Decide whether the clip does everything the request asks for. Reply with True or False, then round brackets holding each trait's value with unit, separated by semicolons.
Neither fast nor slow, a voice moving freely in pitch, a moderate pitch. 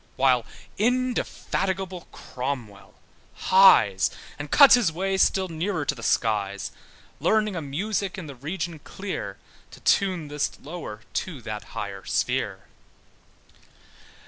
False (120 wpm; 7.2 semitones; 160 Hz)